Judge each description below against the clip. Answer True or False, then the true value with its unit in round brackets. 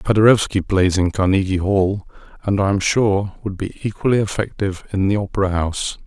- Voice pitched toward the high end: False (100 Hz)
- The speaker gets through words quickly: False (170 wpm)